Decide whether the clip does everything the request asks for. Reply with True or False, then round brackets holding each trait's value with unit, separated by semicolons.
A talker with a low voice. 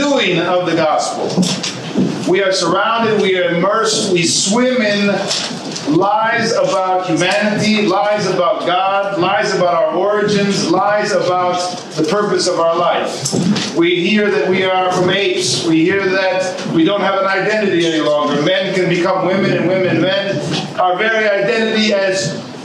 False (190 Hz)